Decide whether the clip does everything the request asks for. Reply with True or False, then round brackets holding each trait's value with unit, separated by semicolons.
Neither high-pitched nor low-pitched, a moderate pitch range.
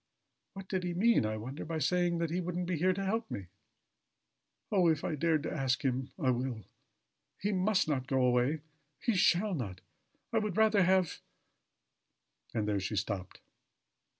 False (165 Hz; 6.5 semitones)